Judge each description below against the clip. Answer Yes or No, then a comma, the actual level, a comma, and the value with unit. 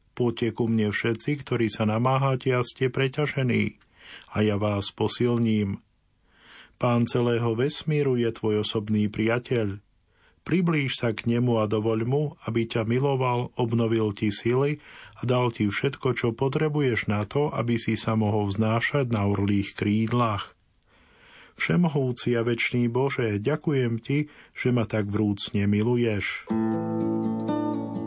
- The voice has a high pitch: No, low, 115 Hz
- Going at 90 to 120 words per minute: No, average, 130 wpm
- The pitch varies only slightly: No, average, 3.0 semitones